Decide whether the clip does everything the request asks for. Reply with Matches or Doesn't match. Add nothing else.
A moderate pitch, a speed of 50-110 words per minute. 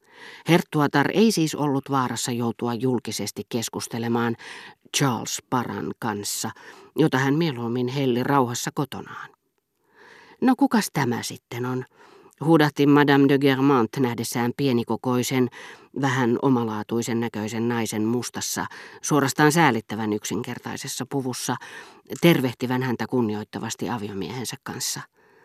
Doesn't match